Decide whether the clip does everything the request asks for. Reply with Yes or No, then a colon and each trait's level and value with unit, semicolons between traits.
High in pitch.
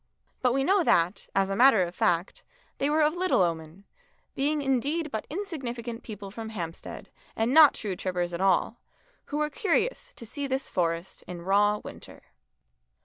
Yes: high, 230 Hz